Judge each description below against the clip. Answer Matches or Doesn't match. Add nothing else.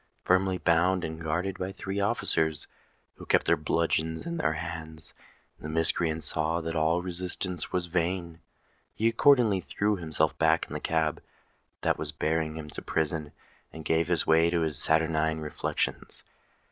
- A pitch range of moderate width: Doesn't match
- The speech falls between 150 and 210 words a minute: Matches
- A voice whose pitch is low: Matches